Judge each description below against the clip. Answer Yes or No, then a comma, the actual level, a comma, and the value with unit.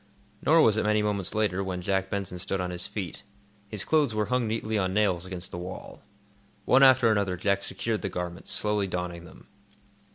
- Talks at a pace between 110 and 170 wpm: No, average, 195 wpm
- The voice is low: Yes, low, 100 Hz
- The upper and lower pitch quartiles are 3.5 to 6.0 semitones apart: No, average, 3.1 semitones